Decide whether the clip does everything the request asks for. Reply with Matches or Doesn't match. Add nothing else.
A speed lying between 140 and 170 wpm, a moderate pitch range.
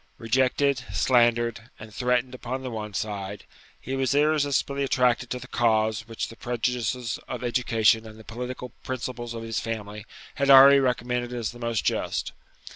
Doesn't match